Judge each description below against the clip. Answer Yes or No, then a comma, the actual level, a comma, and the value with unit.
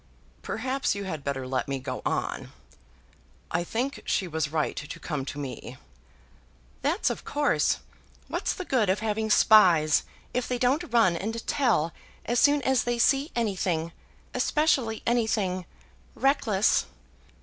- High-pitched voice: Yes, high, 215 Hz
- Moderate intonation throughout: No, wide, 7.9 semitones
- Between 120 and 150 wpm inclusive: Yes, average, 140 wpm